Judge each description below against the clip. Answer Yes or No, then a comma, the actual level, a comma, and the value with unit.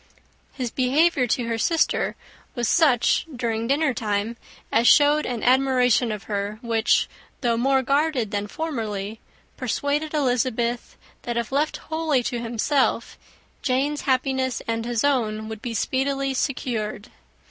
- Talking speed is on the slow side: Yes, slow, 130 wpm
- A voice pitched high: Yes, very high, 250 Hz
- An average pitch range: Yes, average, 3.4 semitones